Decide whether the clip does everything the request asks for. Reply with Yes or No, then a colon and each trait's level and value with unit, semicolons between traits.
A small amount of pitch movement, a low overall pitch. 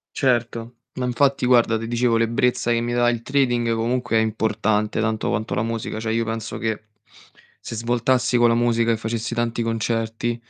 Yes: narrow, 1.2 semitones; low, 115 Hz